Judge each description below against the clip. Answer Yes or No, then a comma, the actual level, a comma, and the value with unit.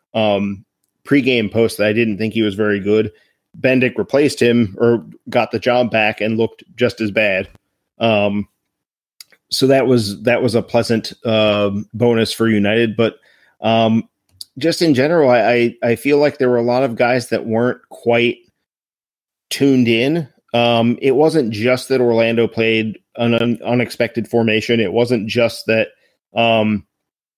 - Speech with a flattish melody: Yes, narrow, 1.9 semitones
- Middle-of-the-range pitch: No, low, 115 Hz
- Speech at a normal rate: Yes, average, 160 wpm